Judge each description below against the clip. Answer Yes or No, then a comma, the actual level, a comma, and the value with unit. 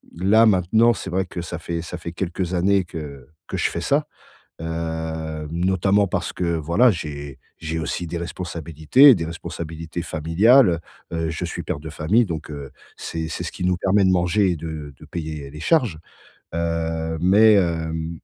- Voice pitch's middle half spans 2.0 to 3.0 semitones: Yes, narrow, 2.6 semitones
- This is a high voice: No, very low, 85 Hz